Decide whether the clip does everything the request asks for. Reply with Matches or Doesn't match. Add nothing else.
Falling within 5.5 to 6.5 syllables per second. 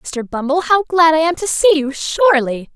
Doesn't match